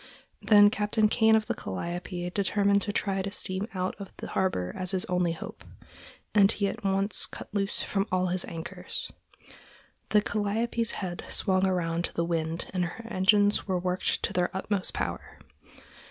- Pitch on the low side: No, high, 190 Hz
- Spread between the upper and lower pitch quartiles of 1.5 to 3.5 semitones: Yes, narrow, 2.4 semitones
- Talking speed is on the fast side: No, average, 170 wpm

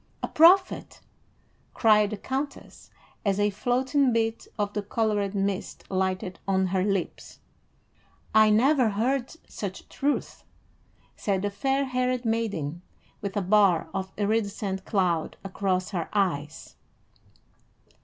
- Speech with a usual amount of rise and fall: Yes, average, 3.3 semitones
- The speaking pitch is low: No, high, 205 Hz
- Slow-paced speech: Yes, slow, 120 wpm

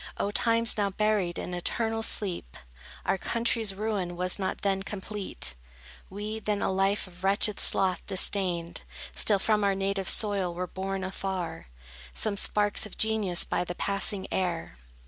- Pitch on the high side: Yes, high, 195 Hz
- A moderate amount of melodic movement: No, narrow, 2.3 semitones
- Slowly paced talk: No, average, 150 wpm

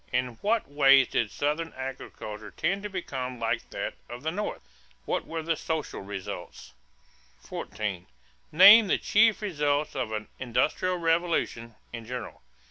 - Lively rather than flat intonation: Yes, wide, 6.3 semitones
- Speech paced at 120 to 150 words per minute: Yes, average, 140 wpm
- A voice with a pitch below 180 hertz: Yes, medium, 140 Hz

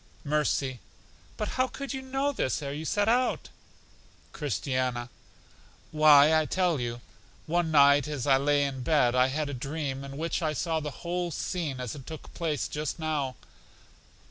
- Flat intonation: No, average, 3.4 semitones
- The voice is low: No, medium, 150 Hz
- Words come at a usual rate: Yes, average, 170 wpm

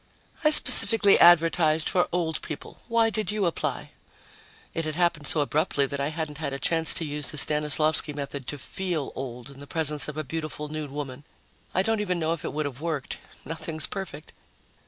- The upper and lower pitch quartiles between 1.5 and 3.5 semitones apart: Yes, average, 2.8 semitones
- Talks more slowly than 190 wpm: No, average, 195 wpm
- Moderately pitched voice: Yes, medium, 155 Hz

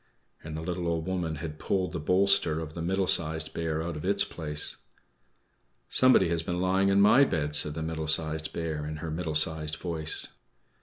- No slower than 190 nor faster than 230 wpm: Yes, average, 195 wpm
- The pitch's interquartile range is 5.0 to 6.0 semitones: No, narrow, 2.4 semitones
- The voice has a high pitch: No, very low, 80 Hz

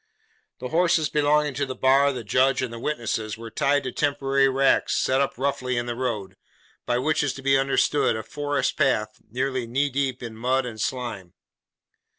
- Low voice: Yes, low, 130 Hz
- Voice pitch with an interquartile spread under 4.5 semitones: Yes, average, 2.7 semitones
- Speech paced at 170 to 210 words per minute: Yes, average, 180 wpm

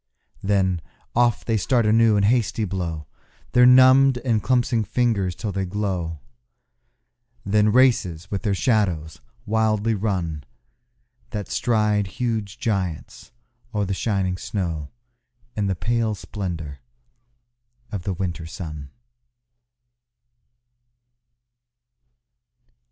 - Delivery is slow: Yes, slow, 100 wpm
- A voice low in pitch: Yes, low, 100 Hz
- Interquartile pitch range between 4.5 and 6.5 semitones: No, average, 3.8 semitones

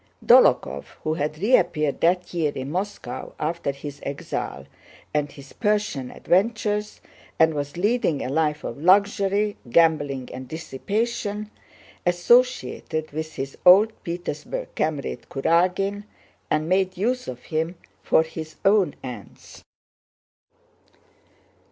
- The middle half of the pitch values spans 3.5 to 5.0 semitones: No, wide, 5.4 semitones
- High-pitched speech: No, medium, 165 Hz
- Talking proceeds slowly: Yes, slow, 115 wpm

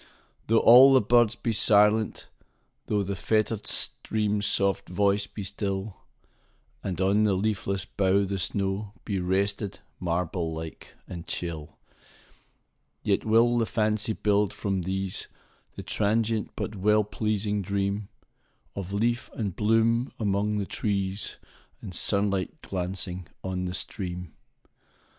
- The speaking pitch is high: No, low, 100 Hz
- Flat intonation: Yes, narrow, 2.2 semitones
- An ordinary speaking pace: No, slow, 105 wpm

